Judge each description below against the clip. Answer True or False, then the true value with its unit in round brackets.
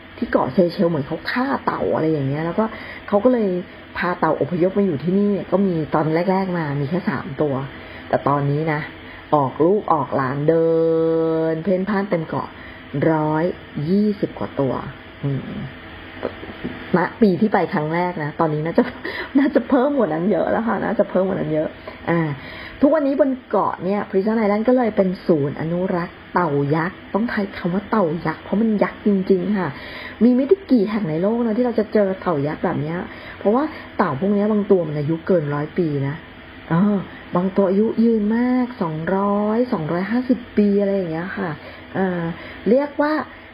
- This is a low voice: False (190 Hz)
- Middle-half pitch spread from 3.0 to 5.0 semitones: True (4.6 semitones)